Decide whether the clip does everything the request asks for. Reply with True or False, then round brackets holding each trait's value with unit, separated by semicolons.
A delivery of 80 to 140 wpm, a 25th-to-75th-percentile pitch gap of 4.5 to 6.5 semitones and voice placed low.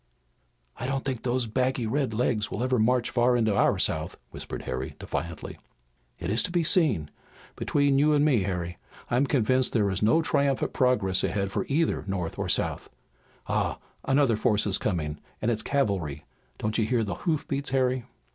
False (180 wpm; 4.9 semitones; 120 Hz)